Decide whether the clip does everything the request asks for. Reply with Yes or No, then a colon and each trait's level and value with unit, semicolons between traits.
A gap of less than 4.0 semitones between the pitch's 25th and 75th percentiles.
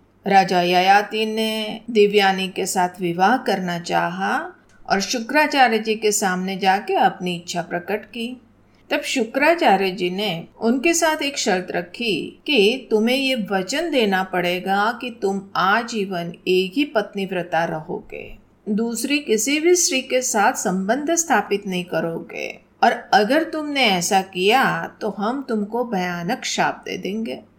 No: average, 5.2 semitones